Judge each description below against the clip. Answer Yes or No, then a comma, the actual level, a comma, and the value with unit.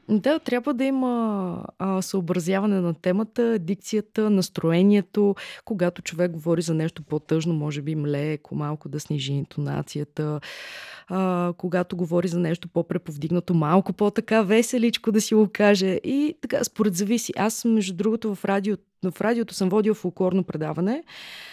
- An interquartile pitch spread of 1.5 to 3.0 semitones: No, average, 4.2 semitones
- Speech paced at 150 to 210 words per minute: No, average, 140 wpm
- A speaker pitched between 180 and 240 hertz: Yes, high, 190 Hz